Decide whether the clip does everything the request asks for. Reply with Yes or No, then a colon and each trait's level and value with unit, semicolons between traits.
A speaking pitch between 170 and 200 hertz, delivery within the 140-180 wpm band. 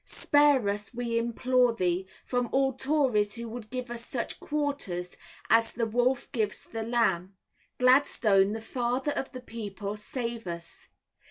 No: high, 235 Hz; average, 150 wpm